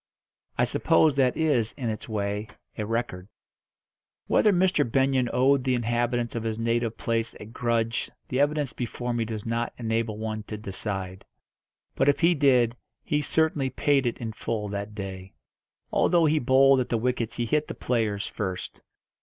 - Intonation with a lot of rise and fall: No, average, 3.5 semitones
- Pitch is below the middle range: Yes, low, 120 Hz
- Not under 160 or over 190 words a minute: Yes, average, 170 wpm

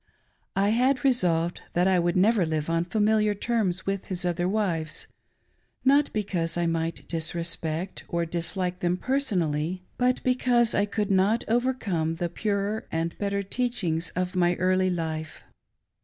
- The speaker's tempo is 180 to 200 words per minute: No, average, 150 wpm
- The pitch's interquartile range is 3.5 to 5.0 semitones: Yes, average, 4.1 semitones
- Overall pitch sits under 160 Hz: No, medium, 185 Hz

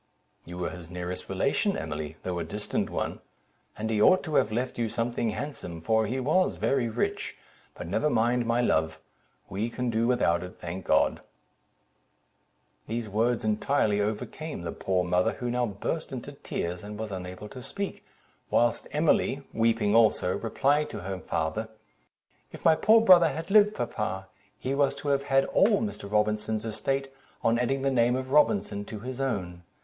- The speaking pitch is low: Yes, low, 115 Hz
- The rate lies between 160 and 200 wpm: Yes, average, 170 wpm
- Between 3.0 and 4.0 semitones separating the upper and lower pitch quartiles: No, wide, 5.6 semitones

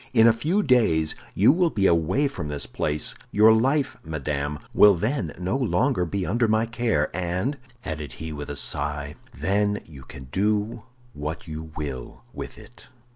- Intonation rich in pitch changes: Yes, wide, 7.2 semitones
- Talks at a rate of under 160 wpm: No, average, 170 wpm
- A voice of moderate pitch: No, very low, 95 Hz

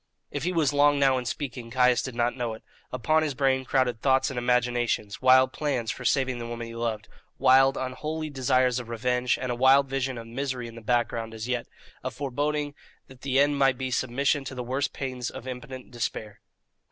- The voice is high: No, low, 130 Hz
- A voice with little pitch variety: Yes, narrow, 2.1 semitones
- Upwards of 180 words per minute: Yes, fast, 205 wpm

